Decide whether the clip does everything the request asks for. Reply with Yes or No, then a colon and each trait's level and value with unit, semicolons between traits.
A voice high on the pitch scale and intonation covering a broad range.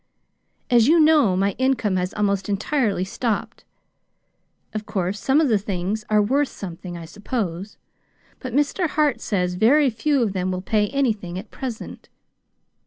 Yes: high, 215 Hz; wide, 5.8 semitones